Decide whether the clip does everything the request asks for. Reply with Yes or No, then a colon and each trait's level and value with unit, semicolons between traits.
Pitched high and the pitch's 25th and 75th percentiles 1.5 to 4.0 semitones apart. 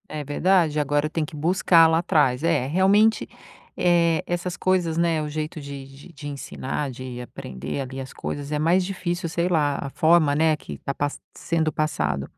No: medium, 155 Hz; average, 3.3 semitones